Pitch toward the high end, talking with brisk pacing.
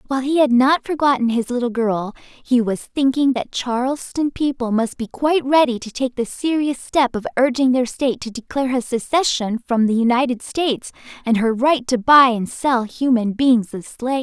No: very high, 250 Hz; average, 195 wpm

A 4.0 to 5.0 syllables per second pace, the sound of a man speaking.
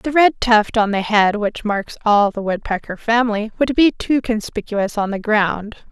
No: 4.5 syllables/s; female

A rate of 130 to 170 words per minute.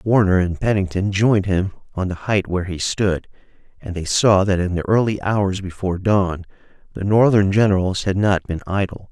No: average, 185 wpm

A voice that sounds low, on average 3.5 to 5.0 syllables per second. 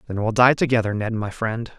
No: low, 115 Hz; 5.6 syllables/s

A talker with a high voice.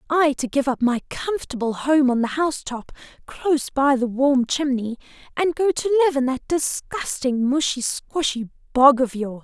Yes: very high, 270 Hz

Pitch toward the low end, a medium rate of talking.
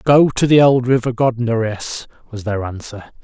Yes: low, 120 Hz; average, 185 wpm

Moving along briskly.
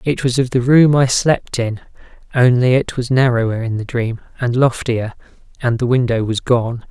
No: average, 190 wpm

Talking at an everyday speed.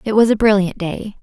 No: fast, 245 wpm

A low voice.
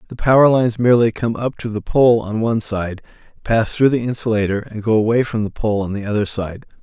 Yes: low, 110 Hz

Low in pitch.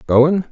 No: medium, 150 Hz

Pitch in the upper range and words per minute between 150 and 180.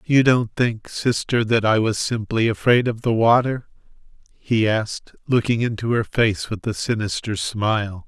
No: low, 110 Hz; average, 165 wpm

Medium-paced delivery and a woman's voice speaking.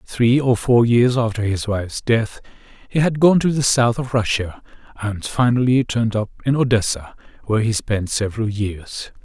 No: average, 175 wpm; male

